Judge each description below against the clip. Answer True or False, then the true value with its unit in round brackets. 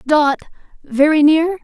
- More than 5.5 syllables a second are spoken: False (4.0 syllables/s)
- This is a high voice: True (305 Hz)